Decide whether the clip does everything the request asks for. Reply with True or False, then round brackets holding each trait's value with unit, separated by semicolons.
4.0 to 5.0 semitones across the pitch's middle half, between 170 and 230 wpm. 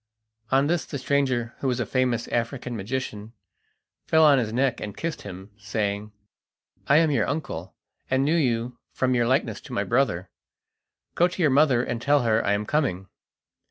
True (4.4 semitones; 180 wpm)